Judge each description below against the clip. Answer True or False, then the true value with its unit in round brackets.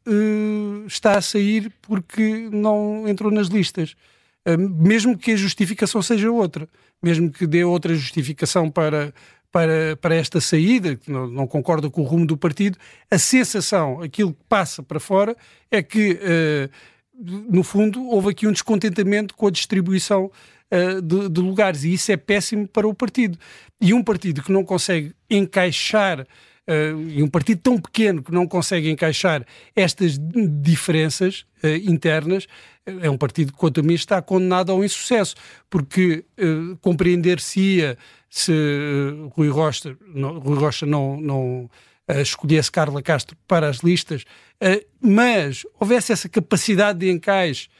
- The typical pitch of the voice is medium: True (180 Hz)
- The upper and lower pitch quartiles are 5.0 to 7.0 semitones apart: False (4.6 semitones)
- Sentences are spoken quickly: False (155 wpm)